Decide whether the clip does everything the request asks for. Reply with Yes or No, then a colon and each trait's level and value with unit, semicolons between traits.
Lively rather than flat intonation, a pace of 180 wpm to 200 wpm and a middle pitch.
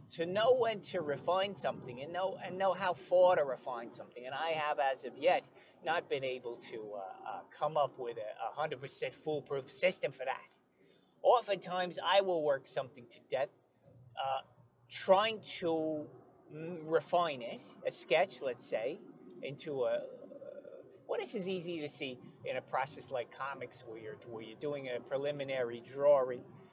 No: wide, 6.2 semitones; average, 170 wpm; medium, 165 Hz